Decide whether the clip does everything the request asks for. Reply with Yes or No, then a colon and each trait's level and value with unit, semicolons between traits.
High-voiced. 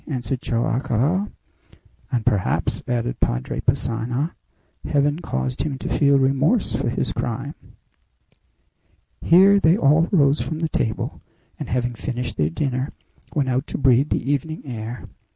No: low, 135 Hz